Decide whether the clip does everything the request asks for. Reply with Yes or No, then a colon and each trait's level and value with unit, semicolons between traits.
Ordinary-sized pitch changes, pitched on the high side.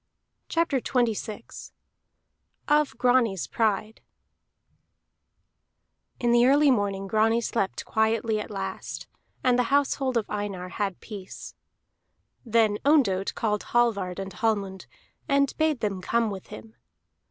Yes: average, 3.9 semitones; high, 220 Hz